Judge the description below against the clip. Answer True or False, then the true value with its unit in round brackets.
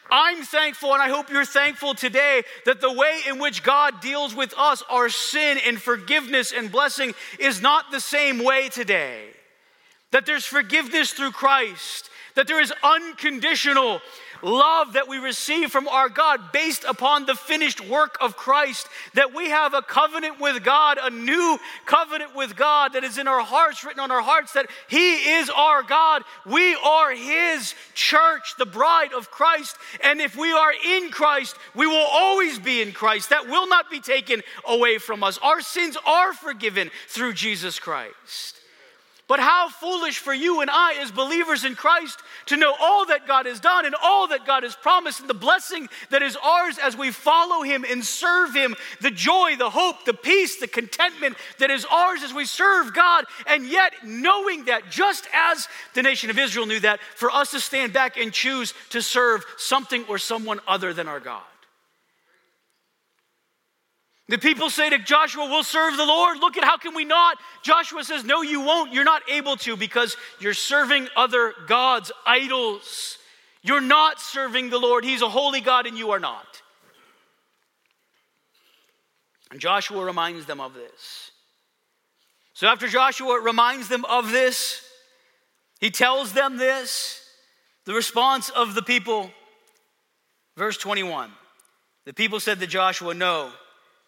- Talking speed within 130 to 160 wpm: False (170 wpm)